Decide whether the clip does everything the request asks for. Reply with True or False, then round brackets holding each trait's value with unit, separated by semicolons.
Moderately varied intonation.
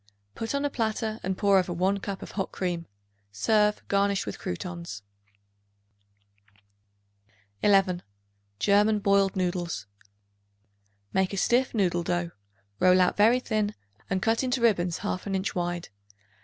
True (3.1 semitones)